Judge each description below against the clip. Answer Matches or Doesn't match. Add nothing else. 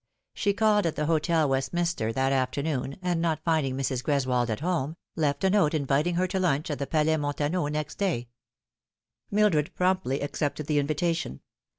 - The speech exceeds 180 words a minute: Doesn't match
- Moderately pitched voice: Matches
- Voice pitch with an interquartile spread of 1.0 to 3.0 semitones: Doesn't match